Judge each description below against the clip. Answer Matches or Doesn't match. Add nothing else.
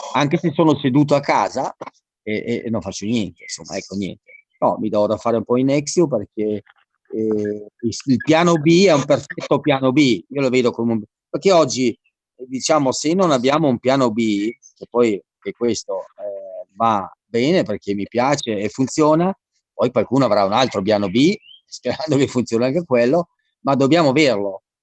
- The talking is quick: Matches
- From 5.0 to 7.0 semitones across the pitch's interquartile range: Matches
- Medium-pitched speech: Doesn't match